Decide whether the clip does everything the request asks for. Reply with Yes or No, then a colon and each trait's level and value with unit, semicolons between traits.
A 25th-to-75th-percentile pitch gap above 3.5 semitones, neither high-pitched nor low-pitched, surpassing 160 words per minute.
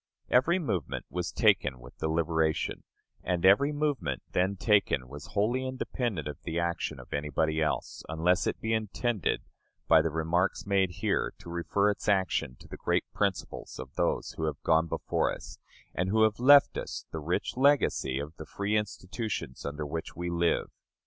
No: average, 5.0 semitones; very low, 90 Hz; average, 170 wpm